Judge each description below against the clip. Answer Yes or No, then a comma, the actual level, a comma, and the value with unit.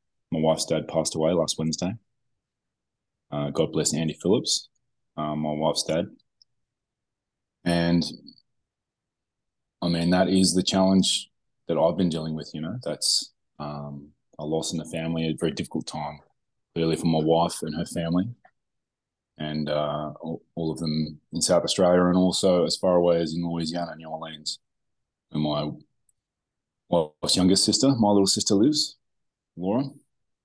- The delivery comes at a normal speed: Yes, average, 150 wpm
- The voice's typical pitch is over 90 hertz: No, very low, 80 Hz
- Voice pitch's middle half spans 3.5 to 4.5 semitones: No, average, 2.9 semitones